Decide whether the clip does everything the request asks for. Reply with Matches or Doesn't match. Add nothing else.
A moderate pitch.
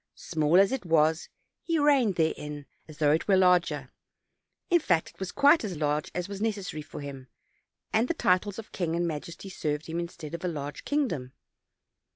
Matches